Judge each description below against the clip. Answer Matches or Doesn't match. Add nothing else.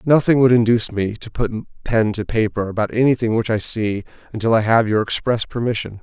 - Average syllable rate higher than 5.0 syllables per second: Matches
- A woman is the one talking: Doesn't match